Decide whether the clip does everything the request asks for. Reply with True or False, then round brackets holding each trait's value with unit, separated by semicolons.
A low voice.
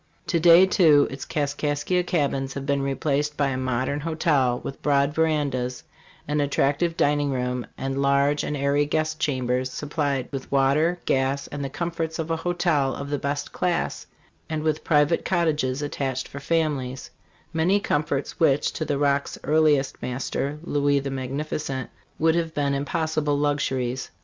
False (145 Hz)